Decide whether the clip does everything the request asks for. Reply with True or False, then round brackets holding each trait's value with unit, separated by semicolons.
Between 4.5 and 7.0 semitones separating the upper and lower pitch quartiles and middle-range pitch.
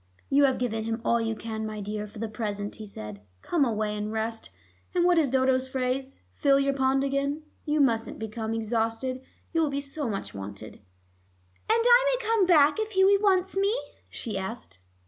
False (5.5 semitones; 255 Hz)